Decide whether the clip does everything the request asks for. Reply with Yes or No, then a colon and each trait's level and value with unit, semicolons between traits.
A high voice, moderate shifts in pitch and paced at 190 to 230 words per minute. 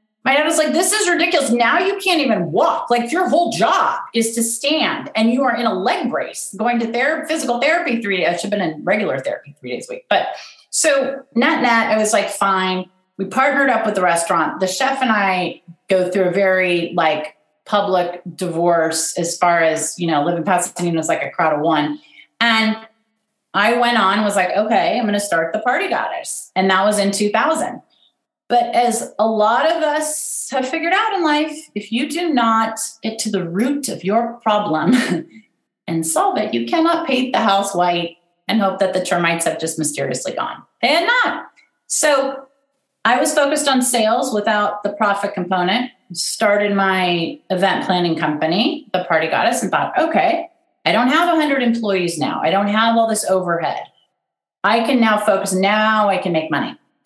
No: high, 220 Hz; wide, 6.5 semitones; average, 195 wpm